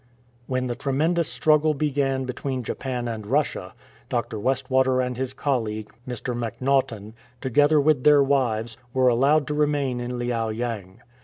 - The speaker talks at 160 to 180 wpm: No, average, 150 wpm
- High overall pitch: No, low, 130 Hz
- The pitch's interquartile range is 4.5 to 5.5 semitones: No, average, 2.8 semitones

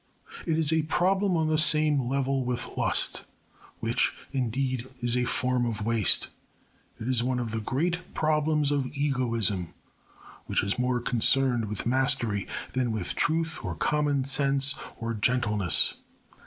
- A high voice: No, low, 130 Hz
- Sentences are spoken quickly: No, average, 145 wpm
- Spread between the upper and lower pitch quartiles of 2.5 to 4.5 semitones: Yes, average, 4.1 semitones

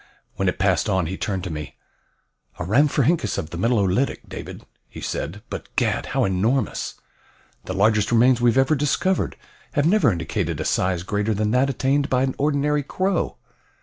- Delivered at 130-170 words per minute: No, average, 180 wpm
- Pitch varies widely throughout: Yes, wide, 6.7 semitones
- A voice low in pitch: Yes, low, 115 Hz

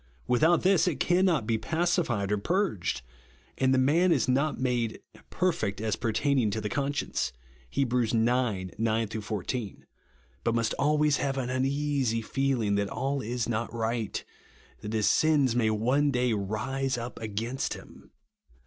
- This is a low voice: Yes, low, 125 Hz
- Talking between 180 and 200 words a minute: No, average, 160 wpm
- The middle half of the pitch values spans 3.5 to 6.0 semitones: Yes, average, 4.2 semitones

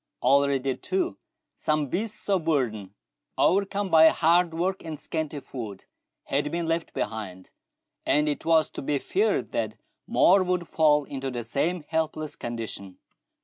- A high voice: No, medium, 155 Hz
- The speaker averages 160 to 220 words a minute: No, average, 145 wpm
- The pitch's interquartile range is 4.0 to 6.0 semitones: Yes, average, 4.3 semitones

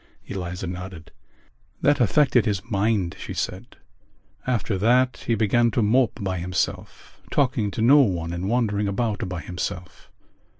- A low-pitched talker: Yes, low, 105 Hz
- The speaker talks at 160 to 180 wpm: No, average, 140 wpm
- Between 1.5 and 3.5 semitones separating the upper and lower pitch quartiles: No, average, 4.5 semitones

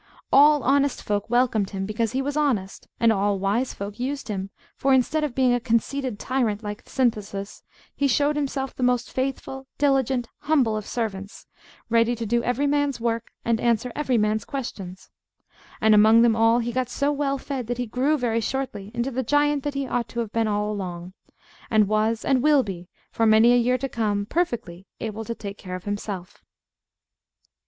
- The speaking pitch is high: Yes, high, 235 Hz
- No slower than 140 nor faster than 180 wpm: No, average, 190 wpm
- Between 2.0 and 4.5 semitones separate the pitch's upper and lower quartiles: Yes, average, 4.0 semitones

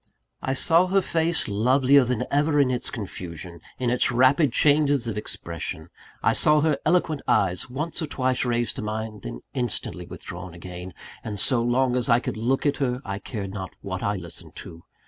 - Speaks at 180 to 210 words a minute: Yes, average, 185 wpm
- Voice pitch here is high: No, low, 120 Hz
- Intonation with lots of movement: Yes, wide, 6.2 semitones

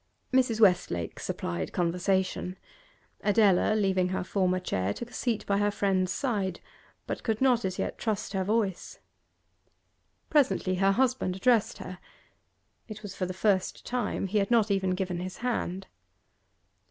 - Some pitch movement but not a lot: Yes, average, 3.1 semitones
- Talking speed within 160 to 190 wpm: No, average, 150 wpm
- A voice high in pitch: Yes, high, 195 Hz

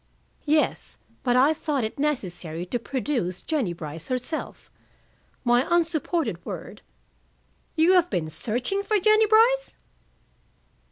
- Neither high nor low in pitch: No, very high, 275 Hz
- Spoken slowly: Yes, slow, 120 wpm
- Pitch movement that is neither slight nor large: No, wide, 7.9 semitones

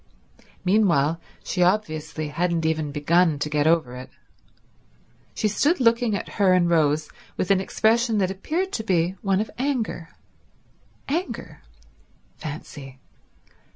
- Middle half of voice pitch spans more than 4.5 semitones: Yes, wide, 5.5 semitones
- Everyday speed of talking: No, slow, 125 wpm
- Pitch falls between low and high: Yes, medium, 180 Hz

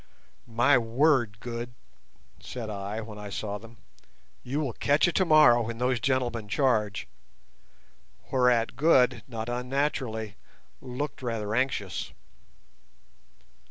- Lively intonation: No, average, 3.0 semitones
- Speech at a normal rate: No, slow, 110 wpm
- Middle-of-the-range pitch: No, low, 120 Hz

